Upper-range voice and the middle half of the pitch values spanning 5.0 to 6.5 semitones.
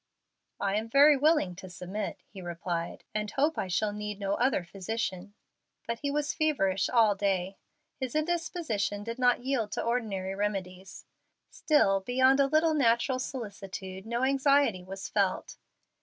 Yes: high, 215 Hz; wide, 5.6 semitones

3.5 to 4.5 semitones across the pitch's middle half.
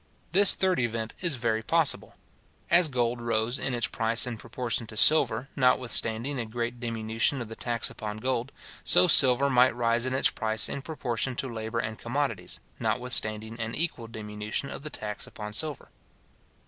No: average, 2.9 semitones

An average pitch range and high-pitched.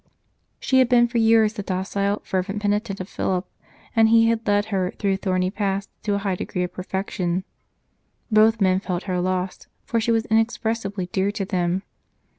Yes: average, 3.0 semitones; high, 200 Hz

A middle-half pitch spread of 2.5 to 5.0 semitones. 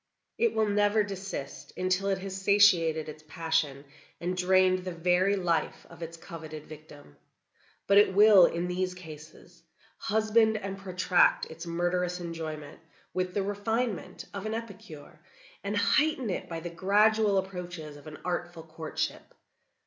Yes: average, 3.3 semitones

